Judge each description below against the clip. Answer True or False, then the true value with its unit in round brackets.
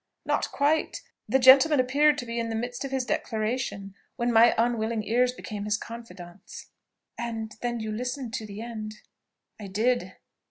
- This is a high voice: True (235 Hz)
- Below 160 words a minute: False (165 wpm)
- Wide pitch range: False (2.7 semitones)